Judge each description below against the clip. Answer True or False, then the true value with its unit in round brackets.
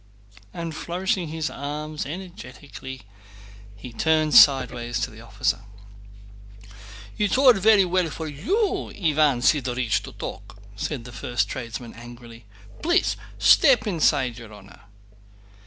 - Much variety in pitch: True (6.4 semitones)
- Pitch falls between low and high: True (145 Hz)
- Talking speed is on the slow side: True (120 wpm)